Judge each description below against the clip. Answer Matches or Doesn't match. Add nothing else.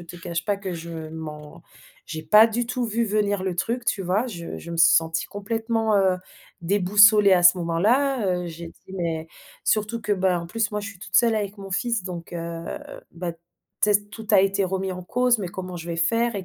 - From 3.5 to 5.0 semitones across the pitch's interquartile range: Matches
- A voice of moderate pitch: Doesn't match